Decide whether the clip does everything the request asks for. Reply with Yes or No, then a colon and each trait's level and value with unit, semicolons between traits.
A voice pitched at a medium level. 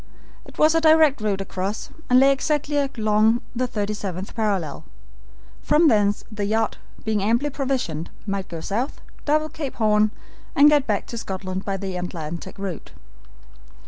No: high, 215 Hz